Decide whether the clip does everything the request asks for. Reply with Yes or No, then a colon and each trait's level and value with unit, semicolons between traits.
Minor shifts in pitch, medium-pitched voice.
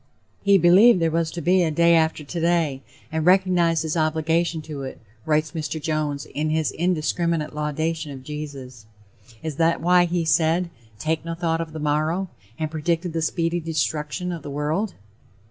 Yes: narrow, 1.9 semitones; medium, 160 Hz